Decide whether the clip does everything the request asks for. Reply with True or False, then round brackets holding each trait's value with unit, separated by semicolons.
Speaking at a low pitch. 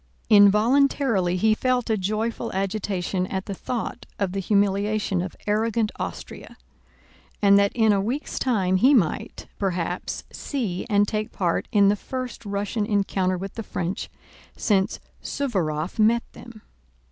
False (205 Hz)